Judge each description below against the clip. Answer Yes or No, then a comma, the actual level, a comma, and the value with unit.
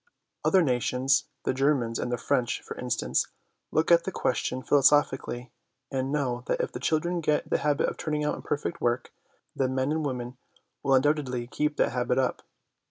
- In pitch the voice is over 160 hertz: No, low, 135 Hz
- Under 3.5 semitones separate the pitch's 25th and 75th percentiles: Yes, average, 3.1 semitones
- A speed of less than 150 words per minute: No, average, 175 wpm